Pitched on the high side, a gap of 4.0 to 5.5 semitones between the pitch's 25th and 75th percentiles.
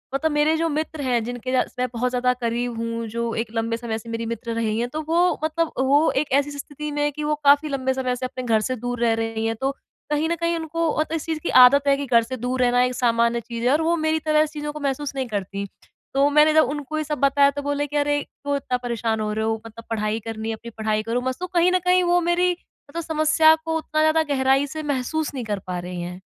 Yes: very high, 265 Hz; average, 4.8 semitones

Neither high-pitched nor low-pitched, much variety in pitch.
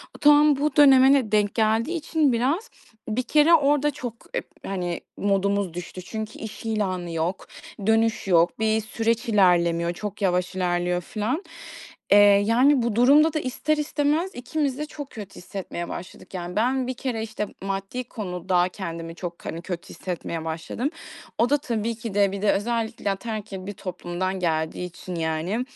No: high, 215 Hz; wide, 5.9 semitones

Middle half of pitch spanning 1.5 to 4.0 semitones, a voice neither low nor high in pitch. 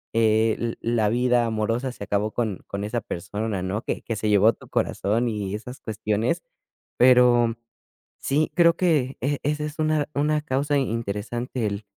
No: average, 3.7 semitones; low, 115 Hz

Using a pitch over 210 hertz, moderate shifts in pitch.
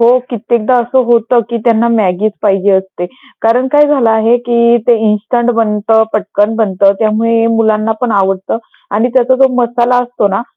No: high, 225 Hz; narrow, 2.2 semitones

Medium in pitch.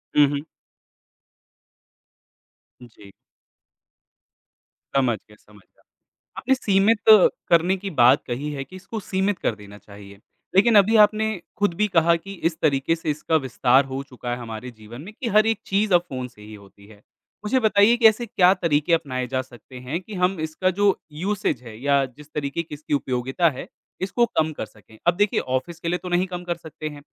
Yes: medium, 160 Hz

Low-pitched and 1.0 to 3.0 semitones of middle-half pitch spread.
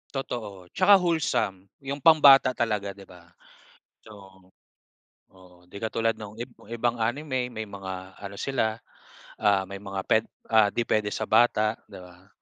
No: low, 110 Hz; average, 3.8 semitones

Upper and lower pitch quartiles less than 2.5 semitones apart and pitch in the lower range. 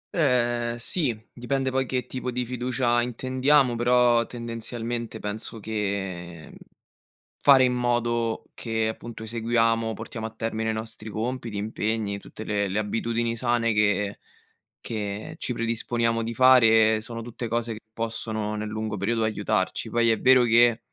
Yes: narrow, 1.7 semitones; low, 115 Hz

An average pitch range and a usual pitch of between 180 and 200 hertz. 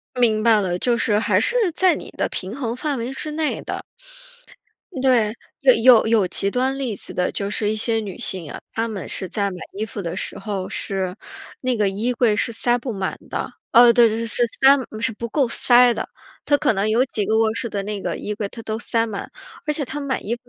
No: average, 3.2 semitones; high, 225 Hz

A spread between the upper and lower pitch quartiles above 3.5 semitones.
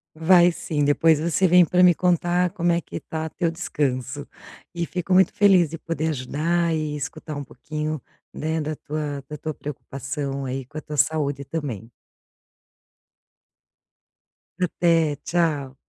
No: average, 2.9 semitones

